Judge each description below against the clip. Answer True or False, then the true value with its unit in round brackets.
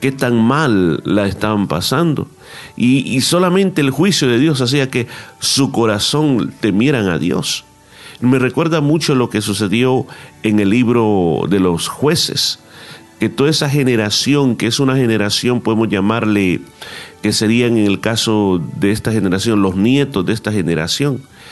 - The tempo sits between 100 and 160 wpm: True (155 wpm)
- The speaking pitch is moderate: False (115 Hz)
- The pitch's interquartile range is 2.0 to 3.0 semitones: False (4.4 semitones)